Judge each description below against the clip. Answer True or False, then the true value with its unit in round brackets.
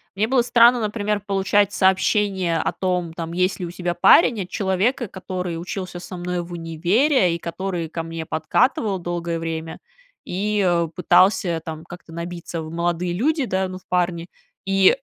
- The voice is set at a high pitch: False (180 Hz)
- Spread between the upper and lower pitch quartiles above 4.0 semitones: False (2.8 semitones)